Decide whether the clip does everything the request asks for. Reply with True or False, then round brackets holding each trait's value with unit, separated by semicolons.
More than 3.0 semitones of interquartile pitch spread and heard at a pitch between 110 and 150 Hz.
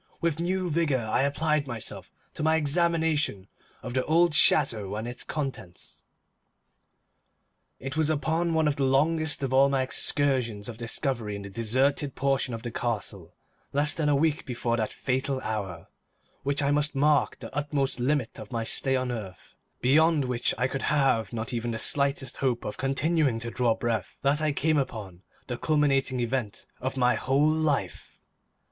True (4.0 semitones; 135 Hz)